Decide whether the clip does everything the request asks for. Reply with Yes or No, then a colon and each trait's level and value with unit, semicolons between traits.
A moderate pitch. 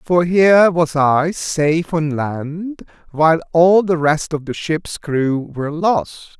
Yes: medium, 160 Hz